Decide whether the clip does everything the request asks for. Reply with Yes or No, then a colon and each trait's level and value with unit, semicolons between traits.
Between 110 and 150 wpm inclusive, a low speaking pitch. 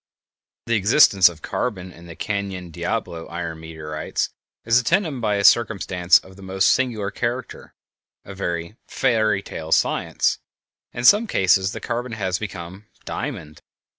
Yes: average, 140 wpm; low, 100 Hz